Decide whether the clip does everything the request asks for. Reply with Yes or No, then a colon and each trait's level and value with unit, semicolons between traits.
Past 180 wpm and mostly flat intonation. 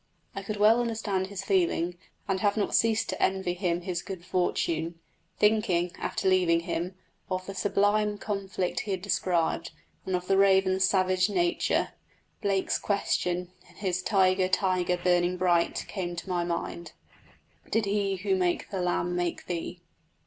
No: average, 155 wpm; narrow, 2.0 semitones